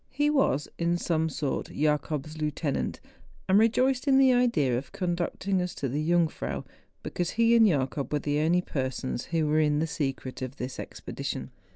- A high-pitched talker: No, medium, 155 Hz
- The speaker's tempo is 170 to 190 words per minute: Yes, average, 180 wpm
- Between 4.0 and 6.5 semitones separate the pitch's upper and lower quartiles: Yes, average, 4.8 semitones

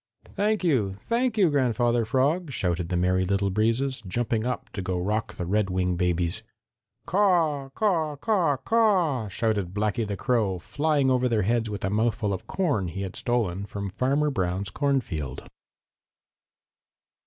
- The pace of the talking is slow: No, average, 150 wpm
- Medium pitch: No, low, 115 Hz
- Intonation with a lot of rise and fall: Yes, wide, 6.9 semitones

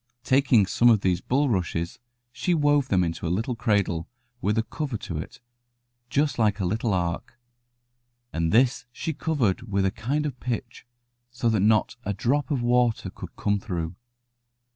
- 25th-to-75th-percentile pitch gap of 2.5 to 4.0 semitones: No, average, 5.0 semitones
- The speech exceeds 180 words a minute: No, average, 165 wpm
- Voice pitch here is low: Yes, low, 115 Hz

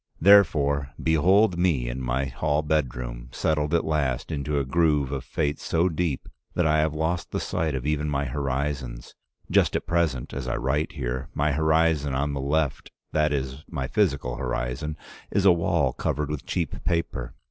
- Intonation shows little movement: No, average, 3.1 semitones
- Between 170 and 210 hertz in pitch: No, very low, 75 Hz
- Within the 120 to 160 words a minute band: No, average, 175 wpm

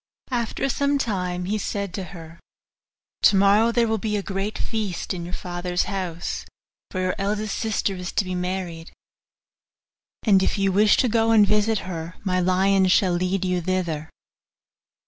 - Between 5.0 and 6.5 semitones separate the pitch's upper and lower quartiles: No, average, 2.8 semitones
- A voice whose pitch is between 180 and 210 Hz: Yes, high, 190 Hz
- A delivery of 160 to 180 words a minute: Yes, average, 165 wpm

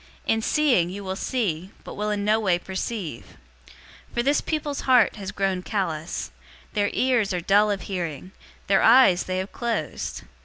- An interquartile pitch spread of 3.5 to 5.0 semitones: Yes, average, 3.8 semitones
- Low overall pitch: No, high, 200 Hz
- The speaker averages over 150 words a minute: Yes, average, 170 wpm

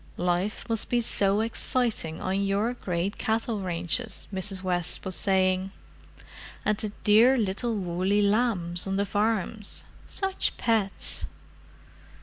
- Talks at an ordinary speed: No, slow, 120 wpm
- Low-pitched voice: No, high, 200 Hz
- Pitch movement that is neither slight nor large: Yes, average, 3.0 semitones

